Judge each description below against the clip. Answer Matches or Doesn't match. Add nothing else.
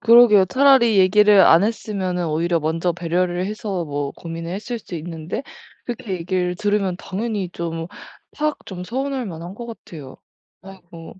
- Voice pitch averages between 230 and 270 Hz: Doesn't match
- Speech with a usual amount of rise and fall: Matches